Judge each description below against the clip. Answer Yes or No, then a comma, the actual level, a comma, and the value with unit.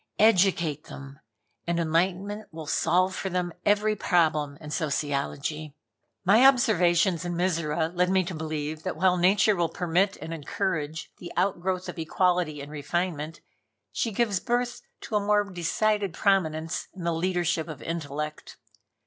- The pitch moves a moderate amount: Yes, average, 3.4 semitones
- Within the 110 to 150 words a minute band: Yes, average, 145 wpm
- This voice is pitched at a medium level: Yes, medium, 175 Hz